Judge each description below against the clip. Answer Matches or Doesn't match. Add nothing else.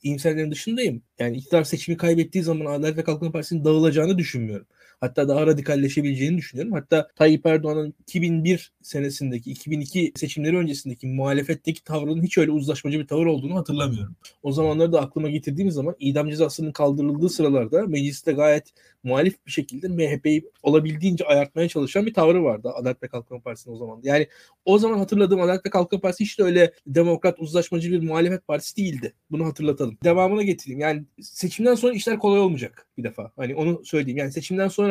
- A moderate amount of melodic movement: Matches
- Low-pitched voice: Doesn't match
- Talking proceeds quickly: Matches